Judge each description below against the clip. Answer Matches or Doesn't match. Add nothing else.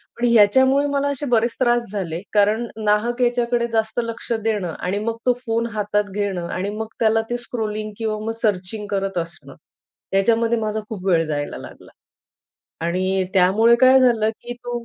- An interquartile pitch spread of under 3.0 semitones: Doesn't match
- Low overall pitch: Doesn't match